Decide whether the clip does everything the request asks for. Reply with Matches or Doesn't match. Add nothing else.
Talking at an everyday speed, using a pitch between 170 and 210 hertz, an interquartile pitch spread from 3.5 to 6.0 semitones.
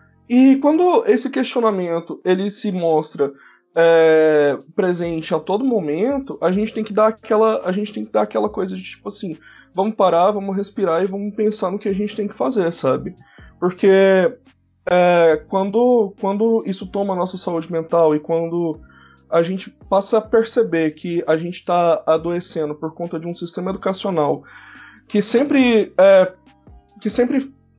Matches